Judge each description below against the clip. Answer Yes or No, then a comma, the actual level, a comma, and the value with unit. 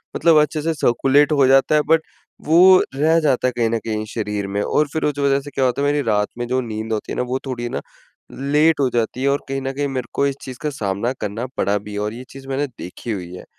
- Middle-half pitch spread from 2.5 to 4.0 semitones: No, average, 4.4 semitones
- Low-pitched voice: Yes, low, 130 Hz